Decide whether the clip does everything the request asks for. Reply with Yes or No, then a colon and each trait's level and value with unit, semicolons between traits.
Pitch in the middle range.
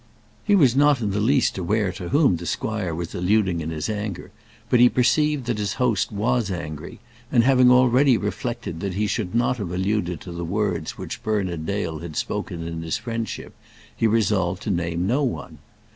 No: low, 105 Hz